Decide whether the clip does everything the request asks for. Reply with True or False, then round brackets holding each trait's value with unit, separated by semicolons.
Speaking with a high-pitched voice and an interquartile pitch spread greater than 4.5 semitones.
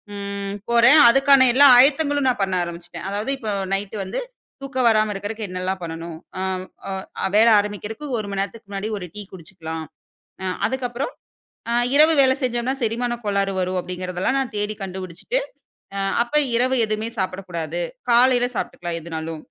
True (205 Hz; 4.9 semitones)